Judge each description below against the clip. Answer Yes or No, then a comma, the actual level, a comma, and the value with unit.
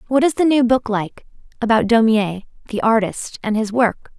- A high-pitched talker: Yes, high, 230 Hz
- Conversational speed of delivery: Yes, average, 185 wpm